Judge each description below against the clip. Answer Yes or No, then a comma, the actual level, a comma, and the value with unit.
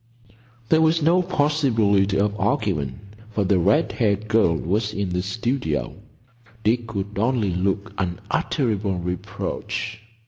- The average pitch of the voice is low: Yes, low, 105 Hz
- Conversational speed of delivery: No, slow, 125 wpm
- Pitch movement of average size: Yes, average, 3.7 semitones